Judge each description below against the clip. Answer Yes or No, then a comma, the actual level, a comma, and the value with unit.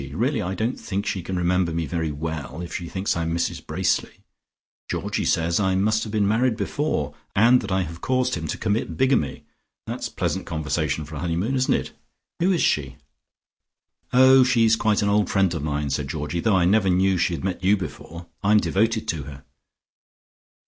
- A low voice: Yes, very low, 95 Hz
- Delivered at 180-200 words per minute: Yes, average, 195 wpm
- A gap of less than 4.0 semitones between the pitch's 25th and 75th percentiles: No, average, 4.9 semitones